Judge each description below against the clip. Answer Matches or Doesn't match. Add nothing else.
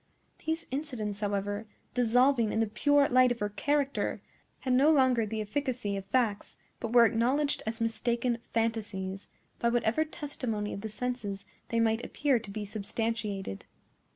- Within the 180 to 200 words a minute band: Doesn't match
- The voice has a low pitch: Doesn't match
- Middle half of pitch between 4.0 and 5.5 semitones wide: Doesn't match